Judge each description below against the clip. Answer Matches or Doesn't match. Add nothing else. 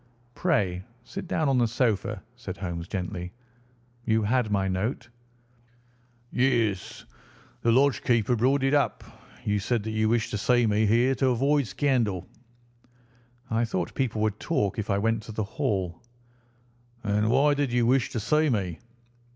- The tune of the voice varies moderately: Matches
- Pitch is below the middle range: Matches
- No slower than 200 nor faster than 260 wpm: Doesn't match